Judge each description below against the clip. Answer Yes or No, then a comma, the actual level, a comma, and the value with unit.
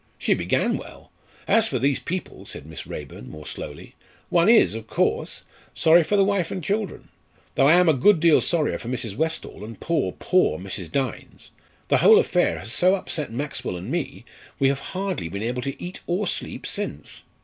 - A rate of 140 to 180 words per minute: No, average, 195 wpm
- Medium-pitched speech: Yes, medium, 145 Hz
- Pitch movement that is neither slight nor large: No, wide, 8.0 semitones